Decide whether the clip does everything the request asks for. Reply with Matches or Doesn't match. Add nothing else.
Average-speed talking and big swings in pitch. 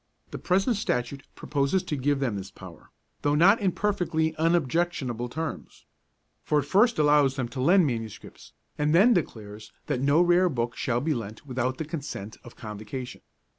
Matches